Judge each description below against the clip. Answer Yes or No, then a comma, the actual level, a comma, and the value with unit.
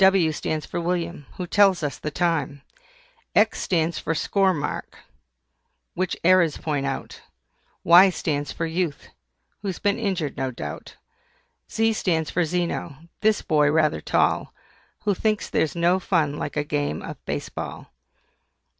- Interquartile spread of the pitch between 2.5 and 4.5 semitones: Yes, average, 3.7 semitones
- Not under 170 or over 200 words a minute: No, average, 145 wpm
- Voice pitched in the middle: Yes, medium, 170 Hz